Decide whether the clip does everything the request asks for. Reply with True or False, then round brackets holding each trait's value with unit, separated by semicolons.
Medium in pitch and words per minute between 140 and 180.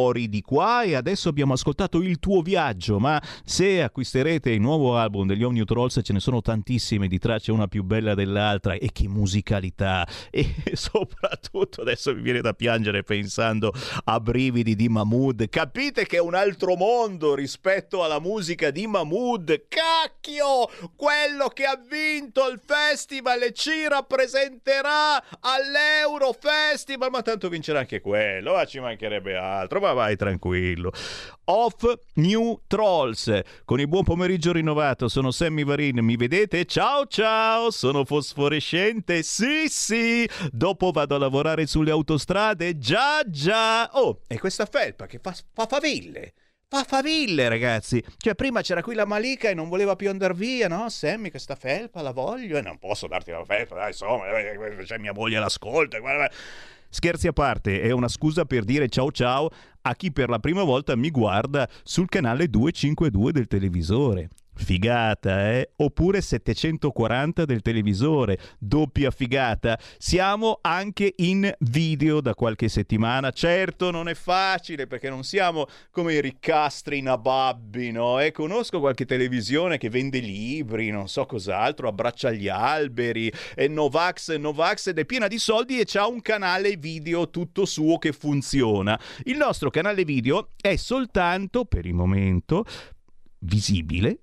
True (155 Hz; 150 wpm)